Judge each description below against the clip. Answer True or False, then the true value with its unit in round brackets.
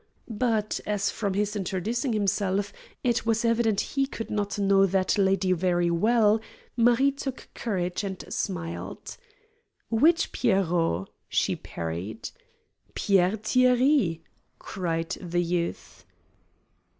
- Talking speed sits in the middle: False (110 wpm)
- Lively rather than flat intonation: False (4.3 semitones)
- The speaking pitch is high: True (200 Hz)